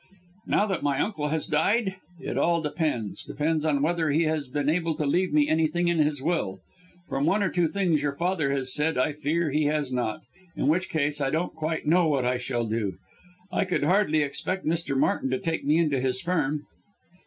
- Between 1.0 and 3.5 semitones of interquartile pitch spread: Yes, average, 3.2 semitones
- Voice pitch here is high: No, medium, 155 Hz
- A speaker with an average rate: No, fast, 210 wpm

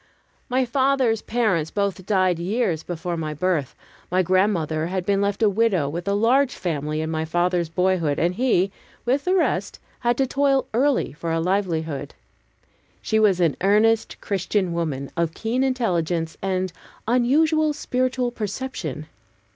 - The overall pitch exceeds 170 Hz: Yes, high, 190 Hz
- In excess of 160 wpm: No, average, 150 wpm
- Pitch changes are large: Yes, wide, 6.2 semitones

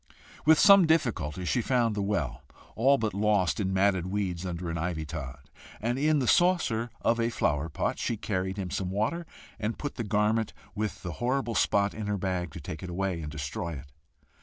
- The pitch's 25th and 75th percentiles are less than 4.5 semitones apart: No, average, 4.9 semitones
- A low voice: Yes, low, 100 Hz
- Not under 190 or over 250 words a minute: Yes, average, 200 wpm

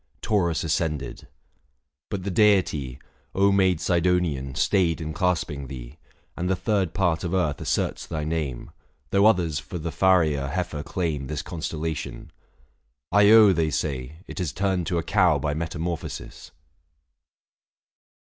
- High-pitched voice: No, very low, 85 Hz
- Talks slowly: Yes, slow, 130 wpm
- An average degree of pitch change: Yes, average, 3.5 semitones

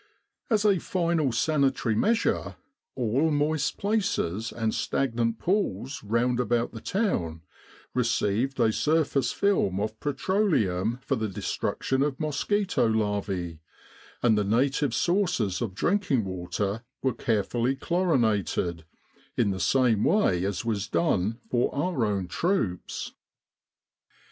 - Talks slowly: Yes, slow, 120 wpm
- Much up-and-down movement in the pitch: Yes, wide, 6.8 semitones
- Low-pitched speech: Yes, low, 120 Hz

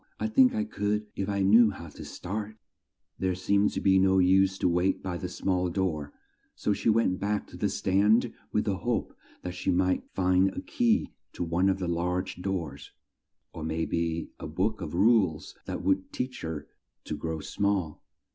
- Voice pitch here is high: No, very low, 95 Hz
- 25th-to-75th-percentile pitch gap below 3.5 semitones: Yes, average, 2.8 semitones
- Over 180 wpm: Yes, average, 190 wpm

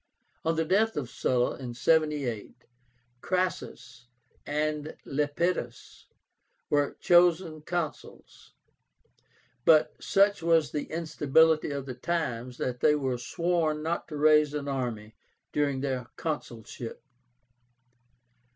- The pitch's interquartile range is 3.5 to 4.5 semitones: Yes, average, 3.9 semitones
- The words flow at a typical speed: No, slow, 105 wpm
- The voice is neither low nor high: Yes, medium, 150 Hz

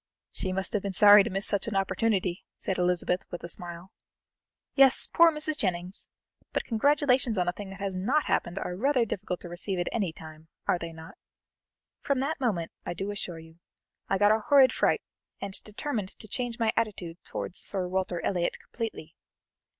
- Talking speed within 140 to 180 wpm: No, average, 190 wpm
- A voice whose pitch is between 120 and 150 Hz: No, high, 195 Hz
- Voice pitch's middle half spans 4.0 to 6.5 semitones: Yes, average, 4.4 semitones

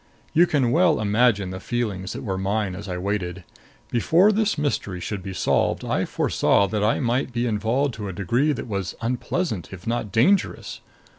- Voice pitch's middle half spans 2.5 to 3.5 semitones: No, average, 4.7 semitones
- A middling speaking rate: Yes, average, 180 wpm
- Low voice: Yes, low, 110 Hz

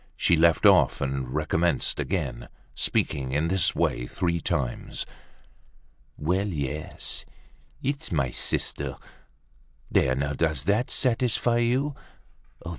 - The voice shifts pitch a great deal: Yes, wide, 6.5 semitones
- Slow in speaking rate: Yes, slow, 110 wpm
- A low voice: Yes, very low, 80 Hz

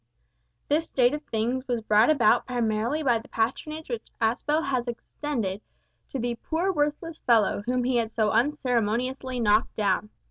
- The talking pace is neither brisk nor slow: Yes, average, 155 wpm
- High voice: Yes, high, 245 Hz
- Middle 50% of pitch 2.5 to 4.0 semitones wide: No, average, 4.4 semitones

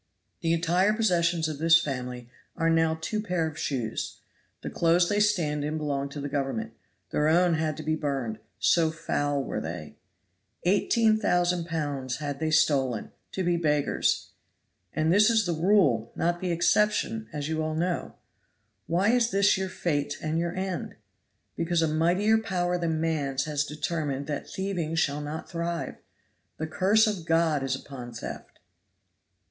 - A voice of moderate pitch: Yes, medium, 165 Hz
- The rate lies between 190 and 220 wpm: No, average, 160 wpm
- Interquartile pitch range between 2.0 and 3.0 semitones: No, average, 3.4 semitones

